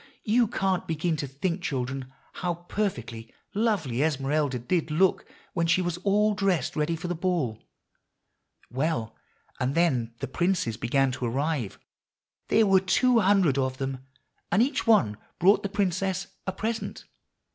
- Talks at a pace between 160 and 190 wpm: No, average, 145 wpm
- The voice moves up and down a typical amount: No, wide, 6.4 semitones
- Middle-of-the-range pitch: Yes, medium, 165 Hz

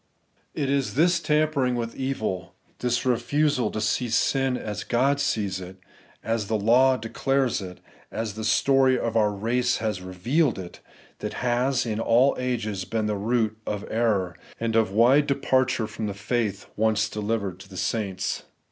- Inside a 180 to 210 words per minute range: No, average, 165 wpm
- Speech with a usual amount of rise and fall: Yes, average, 3.6 semitones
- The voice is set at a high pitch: No, low, 115 Hz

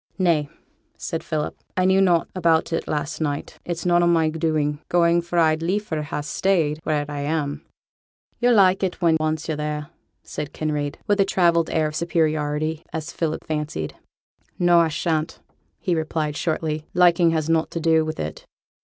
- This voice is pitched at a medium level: Yes, medium, 160 Hz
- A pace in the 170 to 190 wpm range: Yes, average, 175 wpm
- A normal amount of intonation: No, narrow, 2.1 semitones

